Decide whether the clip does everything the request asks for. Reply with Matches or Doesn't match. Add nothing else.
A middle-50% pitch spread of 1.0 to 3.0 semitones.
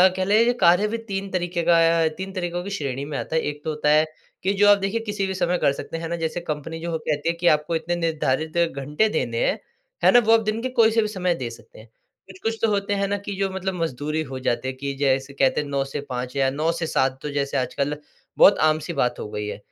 Doesn't match